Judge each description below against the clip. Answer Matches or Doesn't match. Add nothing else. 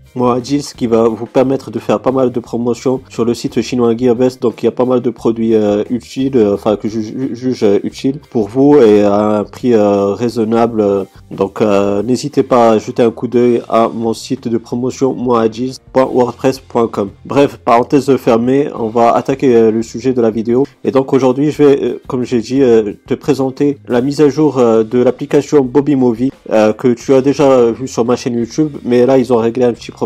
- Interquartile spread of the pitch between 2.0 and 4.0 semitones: Matches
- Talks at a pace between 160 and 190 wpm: Doesn't match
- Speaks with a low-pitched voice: Matches